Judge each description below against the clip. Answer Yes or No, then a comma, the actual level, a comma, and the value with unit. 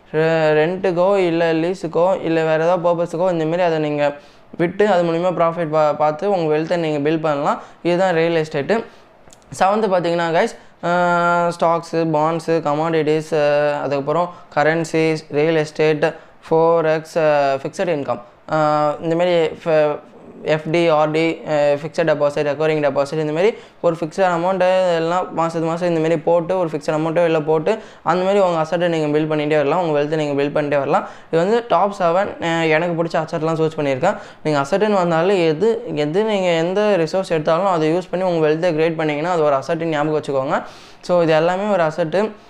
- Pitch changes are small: Yes, narrow, 2.3 semitones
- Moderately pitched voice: Yes, medium, 165 Hz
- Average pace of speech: No, fast, 150 wpm